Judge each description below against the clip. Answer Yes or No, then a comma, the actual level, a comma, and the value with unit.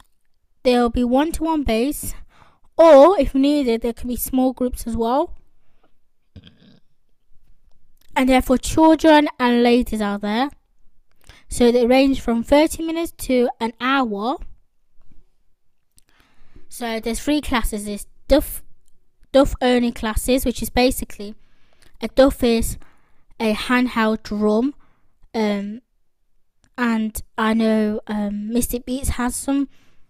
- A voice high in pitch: Yes, high, 245 Hz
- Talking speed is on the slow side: Yes, slow, 115 wpm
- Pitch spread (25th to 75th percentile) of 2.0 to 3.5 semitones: Yes, average, 3.1 semitones